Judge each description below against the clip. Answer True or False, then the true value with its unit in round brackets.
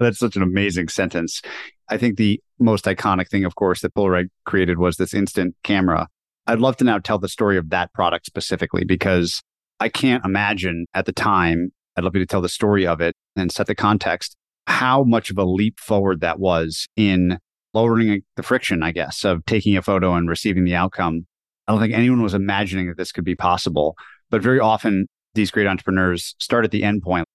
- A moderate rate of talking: False (210 wpm)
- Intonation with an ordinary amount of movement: True (3.0 semitones)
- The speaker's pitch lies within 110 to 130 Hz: False (95 Hz)